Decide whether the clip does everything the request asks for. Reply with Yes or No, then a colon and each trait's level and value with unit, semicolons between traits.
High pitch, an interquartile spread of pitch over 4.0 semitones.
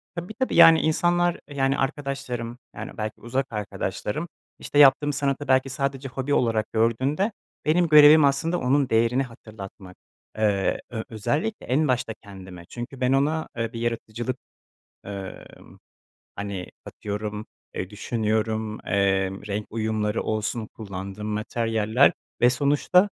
No: low, 120 Hz; average, 4.8 semitones